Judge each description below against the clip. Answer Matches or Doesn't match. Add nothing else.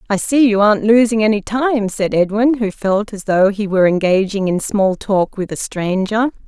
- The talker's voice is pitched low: Doesn't match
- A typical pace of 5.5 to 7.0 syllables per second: Doesn't match